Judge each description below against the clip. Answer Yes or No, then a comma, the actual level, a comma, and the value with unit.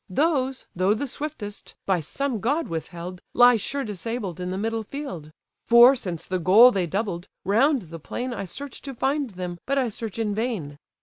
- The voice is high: Yes, high, 220 Hz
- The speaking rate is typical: Yes, average, 185 wpm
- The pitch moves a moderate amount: No, wide, 6.0 semitones